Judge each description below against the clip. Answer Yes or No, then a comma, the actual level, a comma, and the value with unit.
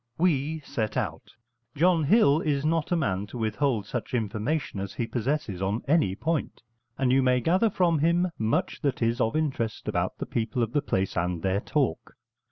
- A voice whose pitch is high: No, low, 130 Hz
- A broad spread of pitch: Yes, wide, 6.3 semitones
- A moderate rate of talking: Yes, average, 185 wpm